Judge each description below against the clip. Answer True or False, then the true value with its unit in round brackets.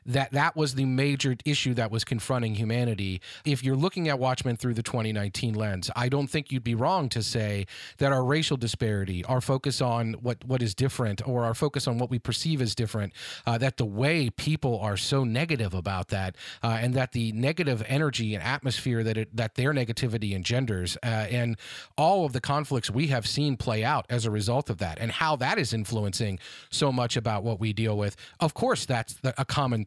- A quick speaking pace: True (210 wpm)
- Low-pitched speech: True (120 Hz)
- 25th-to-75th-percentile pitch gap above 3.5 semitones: False (3.2 semitones)